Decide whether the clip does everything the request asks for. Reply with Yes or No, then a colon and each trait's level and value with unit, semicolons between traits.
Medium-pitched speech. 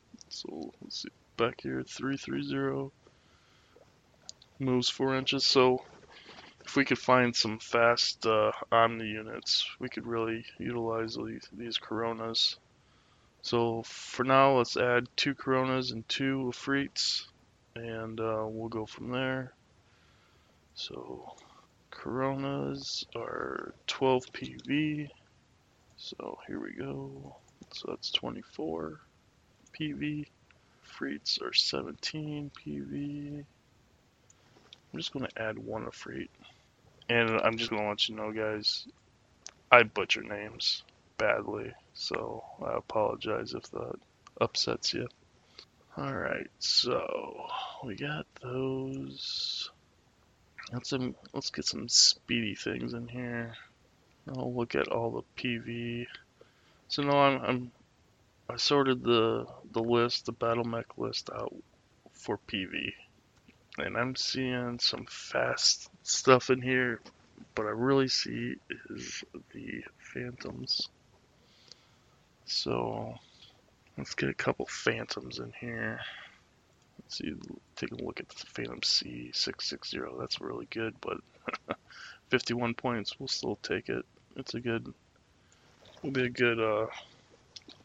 No: low, 120 Hz